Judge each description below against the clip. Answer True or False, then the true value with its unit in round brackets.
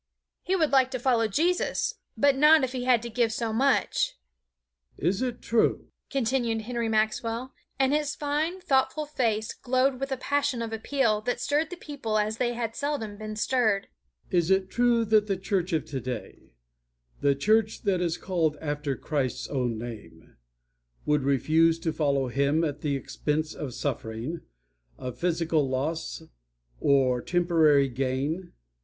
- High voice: True (215 Hz)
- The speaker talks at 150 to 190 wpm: True (155 wpm)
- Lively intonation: True (9.0 semitones)